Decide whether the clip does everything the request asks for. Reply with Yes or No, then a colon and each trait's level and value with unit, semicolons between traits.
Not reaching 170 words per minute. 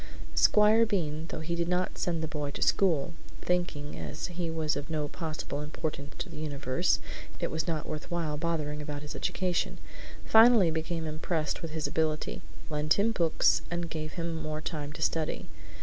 No: average, 180 wpm